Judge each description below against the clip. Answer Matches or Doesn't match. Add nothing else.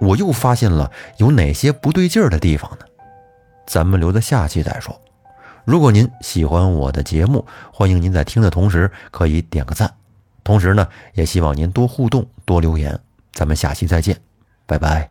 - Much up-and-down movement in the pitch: Matches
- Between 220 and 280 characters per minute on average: Matches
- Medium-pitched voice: Doesn't match